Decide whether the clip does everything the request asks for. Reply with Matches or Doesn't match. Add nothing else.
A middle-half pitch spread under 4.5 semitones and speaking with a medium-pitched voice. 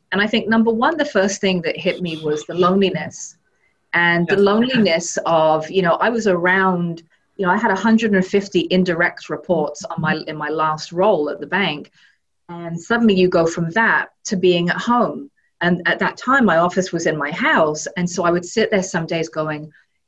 Matches